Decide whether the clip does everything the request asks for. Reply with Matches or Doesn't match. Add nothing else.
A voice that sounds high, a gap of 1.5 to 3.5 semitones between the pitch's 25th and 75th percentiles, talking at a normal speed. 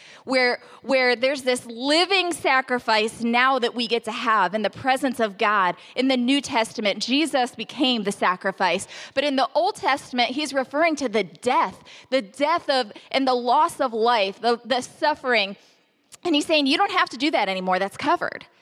Doesn't match